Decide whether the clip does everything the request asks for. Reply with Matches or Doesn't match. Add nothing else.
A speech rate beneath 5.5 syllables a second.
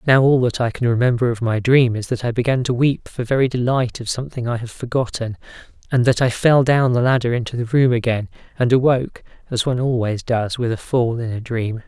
Doesn't match